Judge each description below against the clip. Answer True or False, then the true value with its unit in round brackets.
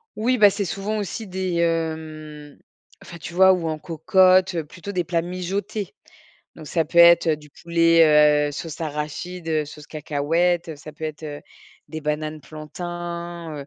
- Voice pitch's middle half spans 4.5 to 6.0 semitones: False (2.8 semitones)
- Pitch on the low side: False (165 Hz)